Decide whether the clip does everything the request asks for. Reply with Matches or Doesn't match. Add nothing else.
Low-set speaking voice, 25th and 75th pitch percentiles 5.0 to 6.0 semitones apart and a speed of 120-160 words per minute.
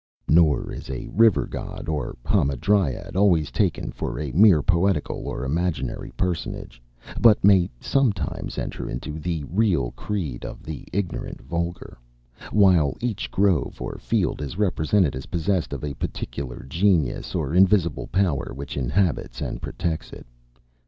Matches